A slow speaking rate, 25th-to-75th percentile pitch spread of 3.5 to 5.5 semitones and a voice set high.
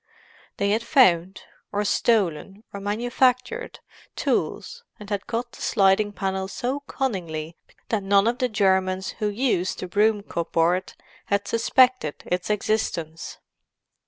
Yes: slow, 130 wpm; average, 3.8 semitones; high, 205 Hz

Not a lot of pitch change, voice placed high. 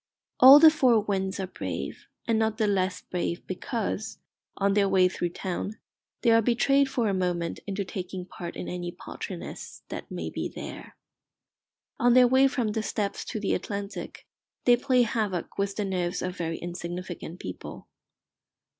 No: average, 4.0 semitones; high, 200 Hz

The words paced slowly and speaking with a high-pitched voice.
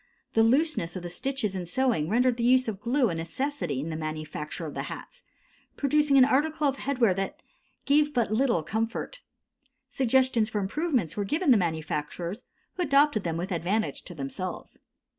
No: average, 175 wpm; high, 225 Hz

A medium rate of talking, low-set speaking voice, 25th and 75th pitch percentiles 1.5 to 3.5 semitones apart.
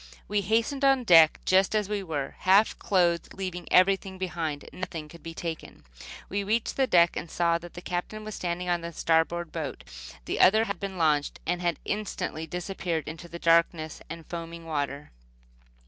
No: average, 175 wpm; medium, 175 Hz; average, 2.9 semitones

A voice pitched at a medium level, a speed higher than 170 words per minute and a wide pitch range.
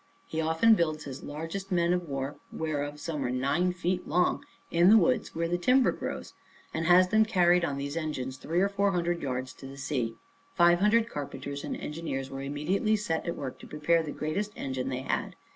No: medium, 165 Hz; fast, 205 wpm; average, 4.2 semitones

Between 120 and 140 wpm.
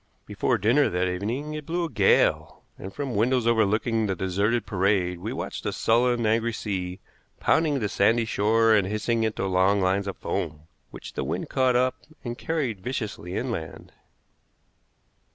No: average, 160 wpm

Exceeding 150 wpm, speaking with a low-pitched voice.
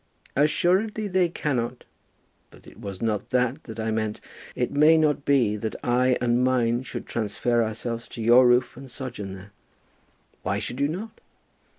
Yes: average, 165 wpm; low, 125 Hz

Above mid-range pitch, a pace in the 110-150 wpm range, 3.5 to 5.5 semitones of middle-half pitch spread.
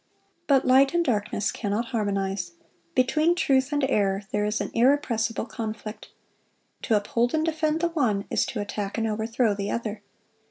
No: high, 225 Hz; average, 160 wpm; average, 4.6 semitones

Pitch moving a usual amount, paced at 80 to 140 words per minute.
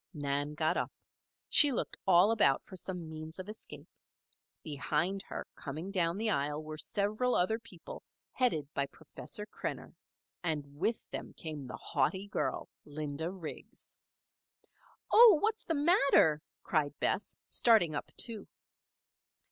No: wide, 6.1 semitones; slow, 135 wpm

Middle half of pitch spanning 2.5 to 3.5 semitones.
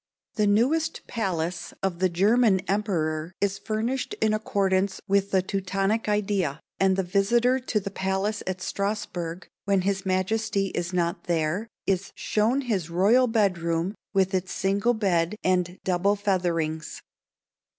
Yes: average, 2.8 semitones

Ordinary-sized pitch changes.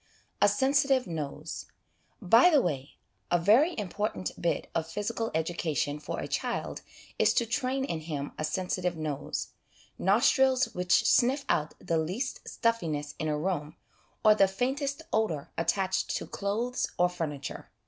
No: wide, 7.0 semitones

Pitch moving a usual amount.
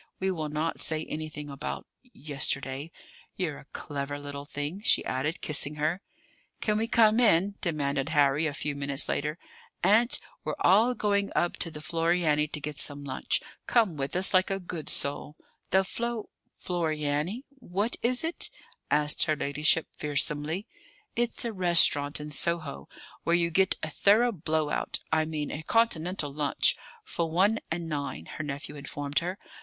Yes: average, 4.6 semitones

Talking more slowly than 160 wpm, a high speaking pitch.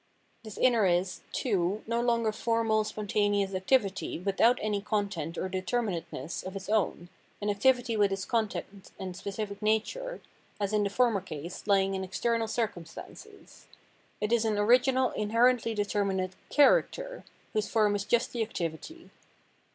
Yes: average, 145 wpm; high, 210 Hz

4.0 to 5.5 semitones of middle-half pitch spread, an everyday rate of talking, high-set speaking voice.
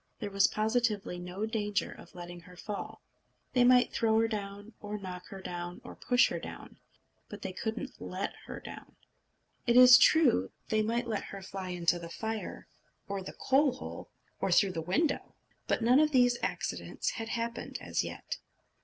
Yes: average, 4.3 semitones; average, 180 wpm; high, 215 Hz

